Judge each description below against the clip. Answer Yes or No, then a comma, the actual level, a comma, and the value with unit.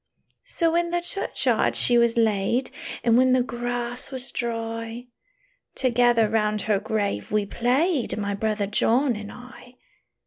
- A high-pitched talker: Yes, high, 235 Hz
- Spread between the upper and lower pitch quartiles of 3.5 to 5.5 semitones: No, average, 2.8 semitones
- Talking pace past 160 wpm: No, average, 140 wpm